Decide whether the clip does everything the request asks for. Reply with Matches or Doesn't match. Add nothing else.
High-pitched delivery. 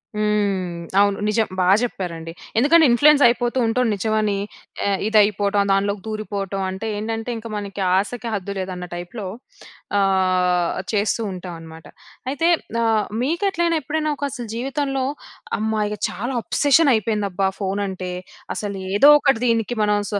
Matches